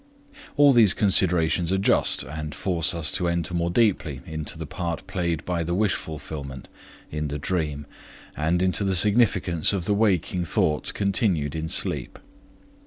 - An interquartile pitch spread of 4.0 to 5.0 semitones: No, average, 3.6 semitones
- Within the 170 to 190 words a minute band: No, average, 160 wpm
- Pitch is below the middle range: Yes, very low, 85 Hz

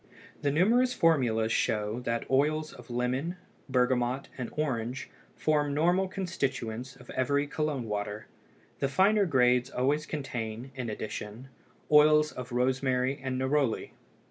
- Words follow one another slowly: Yes, slow, 125 wpm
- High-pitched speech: No, low, 130 Hz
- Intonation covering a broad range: No, average, 3.7 semitones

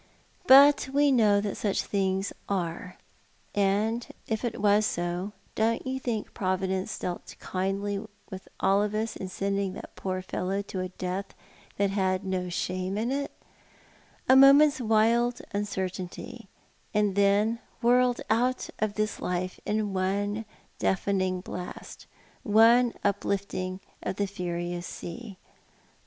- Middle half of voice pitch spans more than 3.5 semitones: No, average, 3.0 semitones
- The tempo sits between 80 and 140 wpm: Yes, slow, 135 wpm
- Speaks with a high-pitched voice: Yes, high, 200 Hz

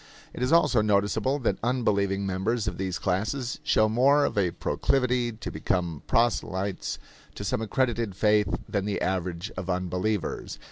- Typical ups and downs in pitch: Yes, average, 4.2 semitones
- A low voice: Yes, low, 105 Hz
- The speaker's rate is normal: Yes, average, 150 wpm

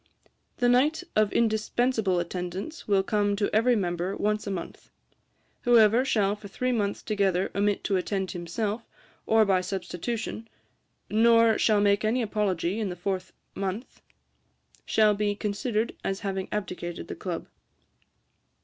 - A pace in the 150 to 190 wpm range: No, average, 140 wpm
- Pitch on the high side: Yes, high, 205 Hz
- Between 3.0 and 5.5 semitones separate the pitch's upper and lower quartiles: No, narrow, 2.6 semitones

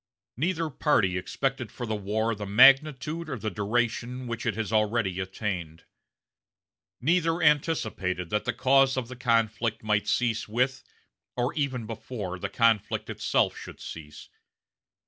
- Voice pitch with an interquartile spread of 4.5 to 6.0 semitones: No, average, 4.0 semitones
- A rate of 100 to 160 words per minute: Yes, average, 140 wpm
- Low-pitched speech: Yes, low, 115 Hz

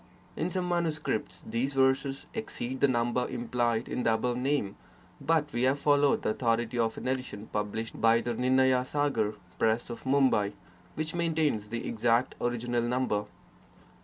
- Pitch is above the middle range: No, low, 125 Hz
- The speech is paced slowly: No, average, 155 wpm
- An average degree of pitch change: Yes, average, 3.4 semitones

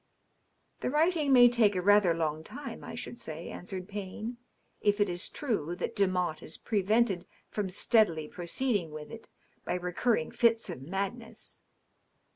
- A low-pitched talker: No, high, 200 Hz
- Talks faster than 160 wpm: Yes, average, 170 wpm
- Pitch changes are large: No, average, 4.9 semitones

